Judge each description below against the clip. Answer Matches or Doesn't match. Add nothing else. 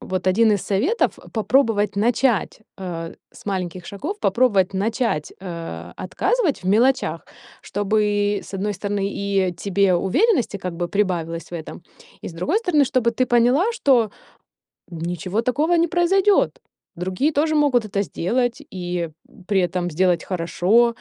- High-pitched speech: Matches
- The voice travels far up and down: Matches